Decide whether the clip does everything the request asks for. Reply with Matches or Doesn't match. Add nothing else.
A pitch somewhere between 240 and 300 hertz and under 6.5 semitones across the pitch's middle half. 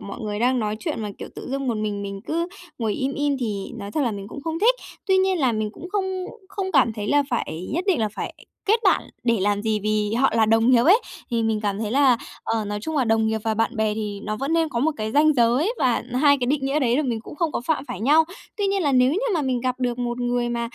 Matches